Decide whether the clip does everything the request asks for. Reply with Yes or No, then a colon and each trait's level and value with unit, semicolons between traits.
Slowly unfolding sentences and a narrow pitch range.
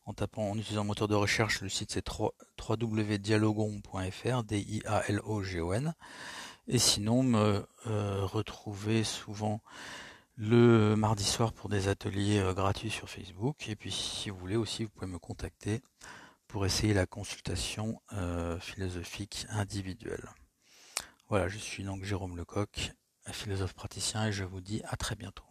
Yes: slow, 135 wpm; narrow, 2.0 semitones